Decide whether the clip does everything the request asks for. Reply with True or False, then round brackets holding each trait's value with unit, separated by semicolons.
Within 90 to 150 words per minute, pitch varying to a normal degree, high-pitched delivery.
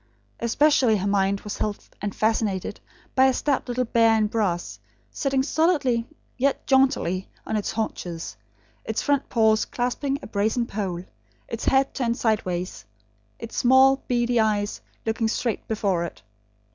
True (145 wpm; 4.1 semitones; 225 Hz)